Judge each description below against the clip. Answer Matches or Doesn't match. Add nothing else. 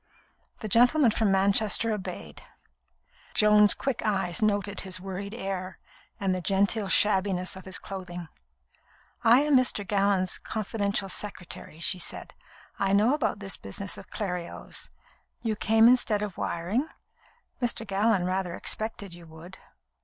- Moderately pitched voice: Doesn't match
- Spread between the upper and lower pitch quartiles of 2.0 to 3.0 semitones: Matches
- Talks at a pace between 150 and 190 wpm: Doesn't match